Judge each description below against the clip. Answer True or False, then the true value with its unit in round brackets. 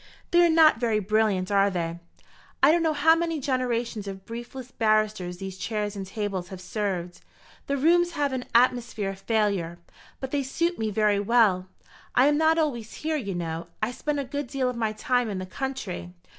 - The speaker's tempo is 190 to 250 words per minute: True (195 wpm)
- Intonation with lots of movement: True (5.9 semitones)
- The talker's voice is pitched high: True (225 Hz)